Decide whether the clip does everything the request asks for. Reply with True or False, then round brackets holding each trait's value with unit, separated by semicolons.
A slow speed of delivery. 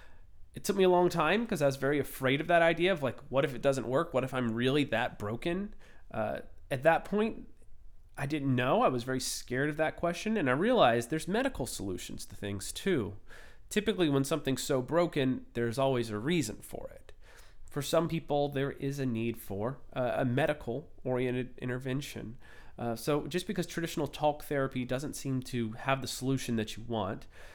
False (195 wpm)